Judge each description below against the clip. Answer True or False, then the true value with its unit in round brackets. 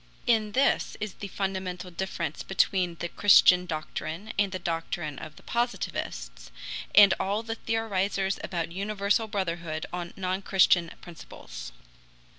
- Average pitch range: True (3.2 semitones)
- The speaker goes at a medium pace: False (130 wpm)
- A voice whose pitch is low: False (185 Hz)